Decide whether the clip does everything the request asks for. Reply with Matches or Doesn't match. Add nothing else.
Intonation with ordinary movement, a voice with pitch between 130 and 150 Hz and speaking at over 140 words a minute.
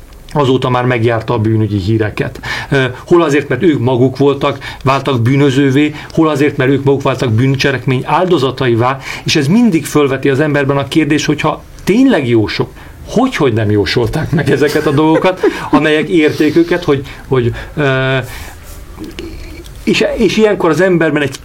Matches